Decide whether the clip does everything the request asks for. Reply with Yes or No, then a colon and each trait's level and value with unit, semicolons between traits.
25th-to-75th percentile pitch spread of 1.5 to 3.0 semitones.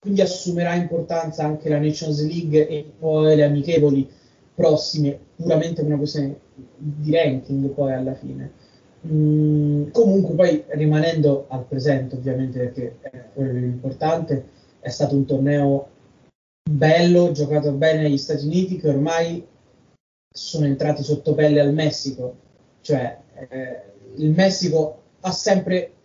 Yes: narrow, 2.6 semitones